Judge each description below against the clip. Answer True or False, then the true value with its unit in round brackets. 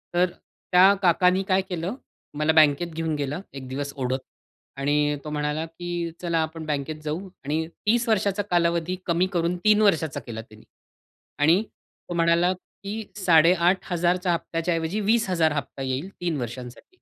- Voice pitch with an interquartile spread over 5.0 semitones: False (3.4 semitones)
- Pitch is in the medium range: True (165 Hz)